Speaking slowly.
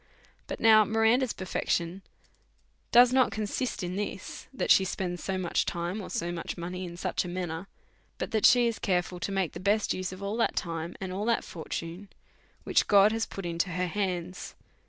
No: average, 195 wpm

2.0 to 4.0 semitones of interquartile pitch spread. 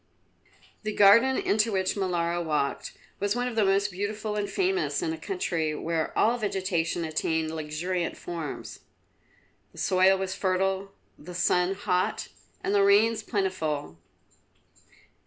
Yes: average, 3.5 semitones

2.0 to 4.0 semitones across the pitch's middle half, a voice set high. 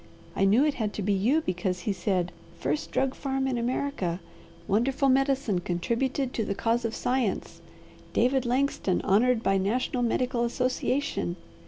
No: average, 5.2 semitones; high, 235 Hz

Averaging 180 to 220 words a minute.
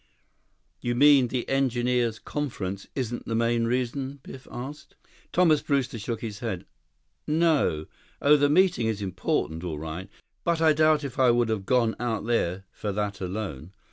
No: average, 160 wpm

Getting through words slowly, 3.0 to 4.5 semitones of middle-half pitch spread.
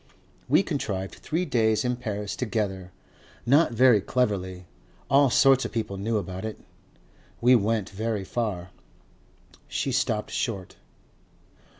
Yes: slow, 120 wpm; average, 4.1 semitones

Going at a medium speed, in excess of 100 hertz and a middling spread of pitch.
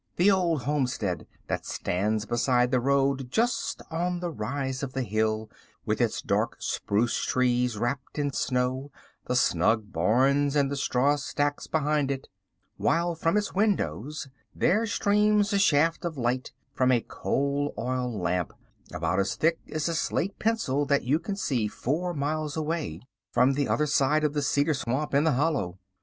Yes: average, 165 wpm; medium, 140 Hz; average, 4.2 semitones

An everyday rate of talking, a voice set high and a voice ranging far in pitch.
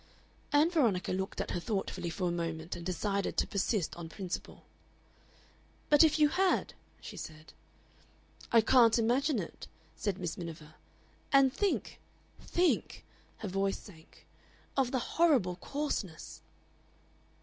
No: slow, 130 wpm; high, 200 Hz; wide, 7.9 semitones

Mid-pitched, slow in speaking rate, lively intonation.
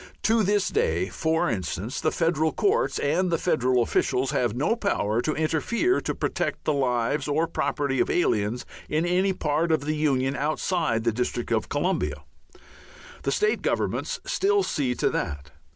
No: medium, 150 Hz; average, 165 wpm; wide, 6.0 semitones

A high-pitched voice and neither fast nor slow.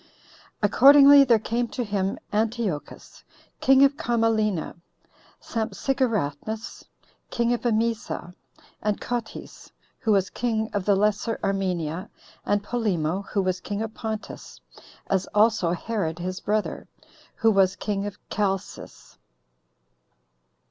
No: high, 210 Hz; slow, 115 wpm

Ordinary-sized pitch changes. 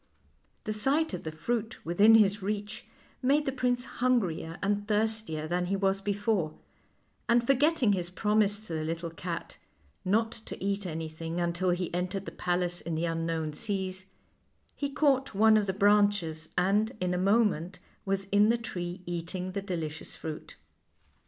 Yes: average, 3.9 semitones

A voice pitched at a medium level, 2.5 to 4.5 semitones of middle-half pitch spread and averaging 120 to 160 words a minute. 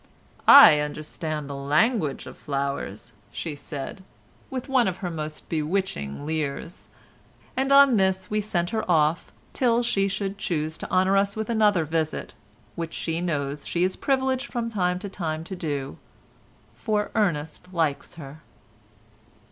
No: medium, 175 Hz; wide, 5.4 semitones; average, 150 wpm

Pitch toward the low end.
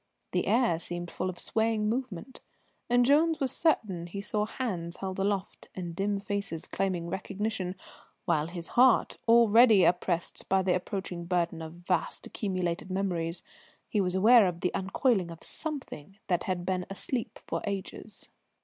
No: high, 190 Hz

